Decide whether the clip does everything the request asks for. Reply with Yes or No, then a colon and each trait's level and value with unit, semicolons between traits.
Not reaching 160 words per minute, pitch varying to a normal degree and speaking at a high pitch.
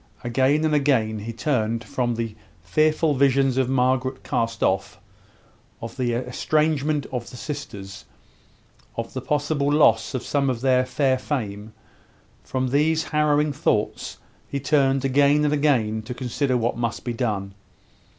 No: average, 145 wpm; average, 3.8 semitones; low, 130 Hz